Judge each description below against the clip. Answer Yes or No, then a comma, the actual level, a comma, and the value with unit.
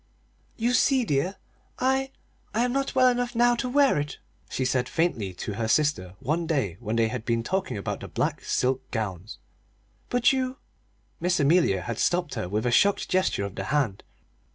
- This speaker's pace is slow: No, average, 190 wpm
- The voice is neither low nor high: Yes, medium, 150 Hz